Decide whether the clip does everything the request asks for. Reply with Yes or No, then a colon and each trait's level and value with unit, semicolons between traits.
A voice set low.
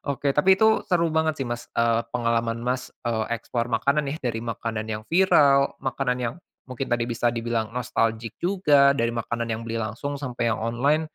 Yes: low, 120 Hz